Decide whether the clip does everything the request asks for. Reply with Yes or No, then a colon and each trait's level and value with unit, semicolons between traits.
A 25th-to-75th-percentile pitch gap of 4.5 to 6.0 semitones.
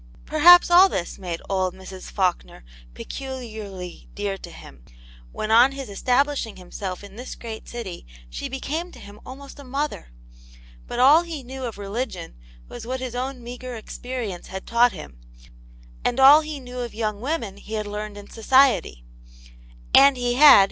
Yes: average, 5.0 semitones